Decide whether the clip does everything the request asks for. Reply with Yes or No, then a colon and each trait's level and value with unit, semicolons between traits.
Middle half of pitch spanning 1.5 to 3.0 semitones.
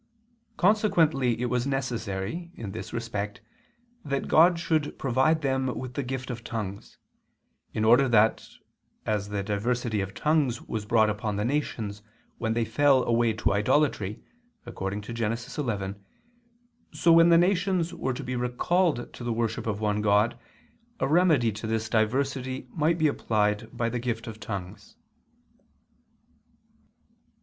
No: average, 4.5 semitones